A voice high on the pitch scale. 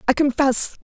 Yes: very high, 270 Hz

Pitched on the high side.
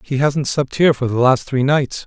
No: low, 135 Hz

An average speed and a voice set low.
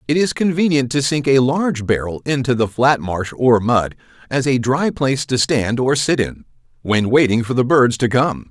No: fast, 210 wpm; low, 130 Hz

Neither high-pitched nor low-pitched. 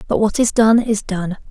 No: high, 215 Hz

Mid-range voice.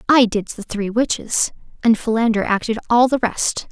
No: high, 225 Hz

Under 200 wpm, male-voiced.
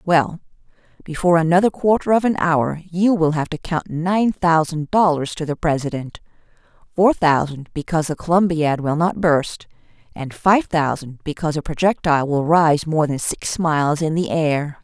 No: average, 165 wpm; female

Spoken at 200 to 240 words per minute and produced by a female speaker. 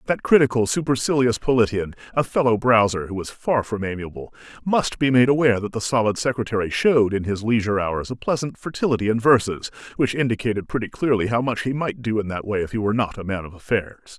No: fast, 205 wpm; male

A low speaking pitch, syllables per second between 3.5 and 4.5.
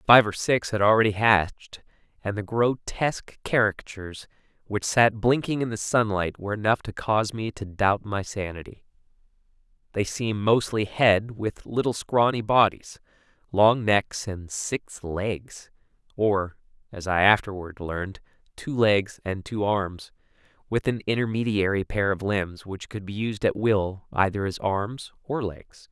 Yes: low, 105 Hz; 4.4 syllables/s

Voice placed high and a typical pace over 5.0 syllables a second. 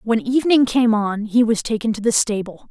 Yes: high, 225 Hz; 5.2 syllables/s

